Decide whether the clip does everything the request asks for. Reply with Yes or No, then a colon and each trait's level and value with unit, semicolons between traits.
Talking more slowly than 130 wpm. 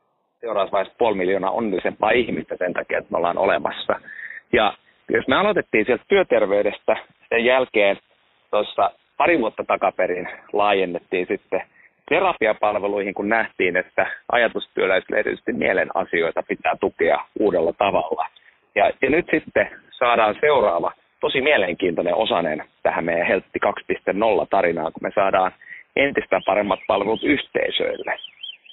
Yes: average, 120 wpm